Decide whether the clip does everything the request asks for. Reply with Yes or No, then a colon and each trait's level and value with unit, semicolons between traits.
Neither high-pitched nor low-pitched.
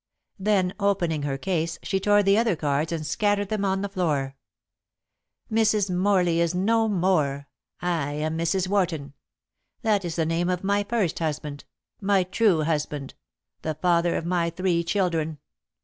Yes: medium, 175 Hz